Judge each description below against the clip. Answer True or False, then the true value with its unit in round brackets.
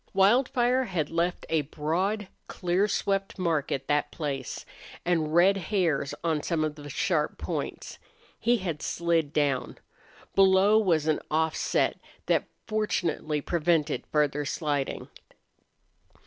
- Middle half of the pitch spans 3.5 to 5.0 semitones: True (4.4 semitones)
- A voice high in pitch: False (165 Hz)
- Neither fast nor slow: False (120 wpm)